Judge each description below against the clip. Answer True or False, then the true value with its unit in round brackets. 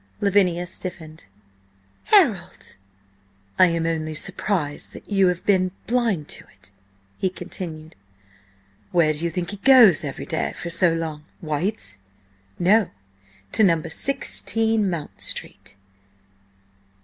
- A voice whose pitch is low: False (175 Hz)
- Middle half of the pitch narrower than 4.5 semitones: True (4.0 semitones)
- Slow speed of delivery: True (115 wpm)